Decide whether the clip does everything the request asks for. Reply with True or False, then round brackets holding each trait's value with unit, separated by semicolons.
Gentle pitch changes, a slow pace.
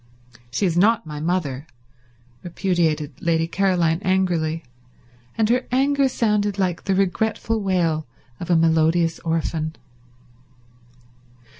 False (3.4 semitones; 110 wpm)